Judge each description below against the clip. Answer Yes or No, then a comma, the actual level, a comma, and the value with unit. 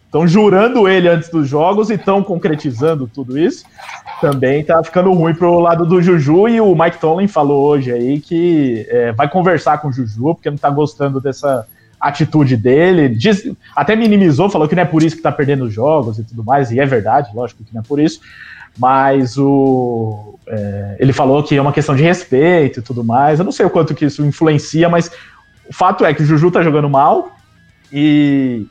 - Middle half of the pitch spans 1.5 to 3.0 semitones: No, average, 4.2 semitones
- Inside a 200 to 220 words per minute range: Yes, fast, 205 wpm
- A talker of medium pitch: Yes, medium, 150 Hz